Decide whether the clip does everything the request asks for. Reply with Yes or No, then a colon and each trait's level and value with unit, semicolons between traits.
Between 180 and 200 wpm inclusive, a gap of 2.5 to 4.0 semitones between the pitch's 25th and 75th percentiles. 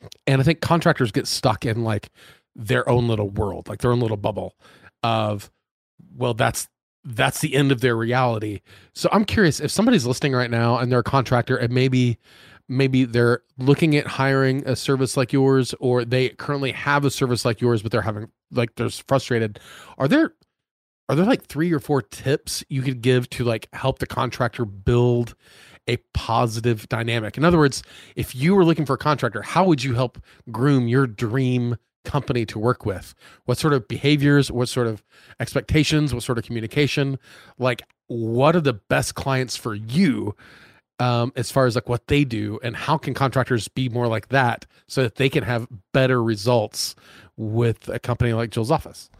Yes: average, 190 wpm; average, 2.8 semitones